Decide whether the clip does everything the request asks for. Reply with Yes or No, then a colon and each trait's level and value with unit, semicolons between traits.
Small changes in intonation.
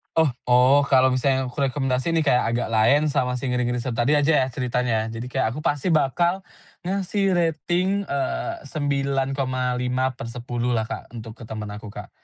No: average, 3.2 semitones